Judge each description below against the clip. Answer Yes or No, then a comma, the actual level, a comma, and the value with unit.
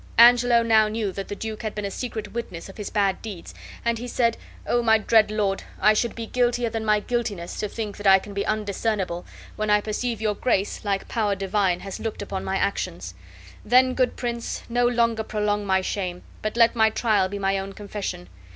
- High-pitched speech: Yes, high, 215 Hz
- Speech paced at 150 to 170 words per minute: No, fast, 205 wpm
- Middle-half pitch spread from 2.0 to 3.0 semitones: Yes, average, 2.7 semitones